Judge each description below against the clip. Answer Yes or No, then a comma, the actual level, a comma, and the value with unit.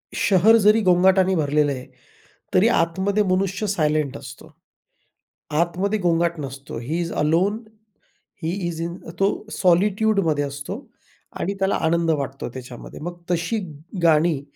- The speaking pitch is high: No, medium, 170 Hz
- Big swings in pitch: No, average, 4.2 semitones